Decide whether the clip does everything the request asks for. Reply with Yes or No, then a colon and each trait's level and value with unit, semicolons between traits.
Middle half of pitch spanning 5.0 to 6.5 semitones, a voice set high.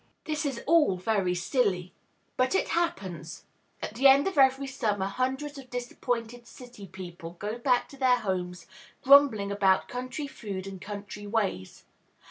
Yes: wide, 5.6 semitones; high, 230 Hz